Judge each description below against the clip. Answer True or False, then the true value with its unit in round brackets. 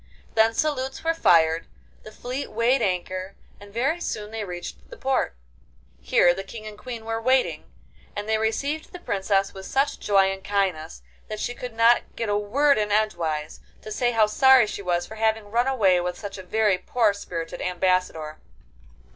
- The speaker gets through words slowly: False (180 wpm)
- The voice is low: False (215 Hz)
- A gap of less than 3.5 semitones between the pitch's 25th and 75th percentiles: False (4.3 semitones)